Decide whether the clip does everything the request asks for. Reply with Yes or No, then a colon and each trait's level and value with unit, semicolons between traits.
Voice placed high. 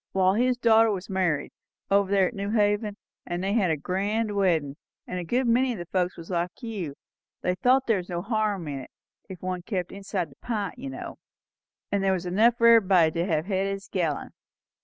Yes: high, 195 Hz